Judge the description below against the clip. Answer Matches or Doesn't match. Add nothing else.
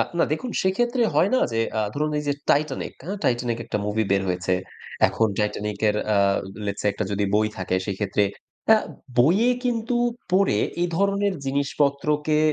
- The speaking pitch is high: Doesn't match